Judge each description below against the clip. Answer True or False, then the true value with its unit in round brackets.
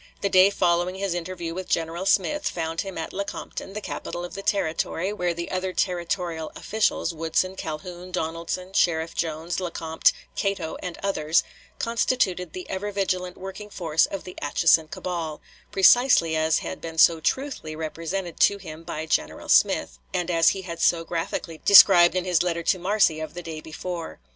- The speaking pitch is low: False (175 Hz)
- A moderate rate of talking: True (170 wpm)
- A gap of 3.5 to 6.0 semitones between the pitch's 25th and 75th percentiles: False (2.5 semitones)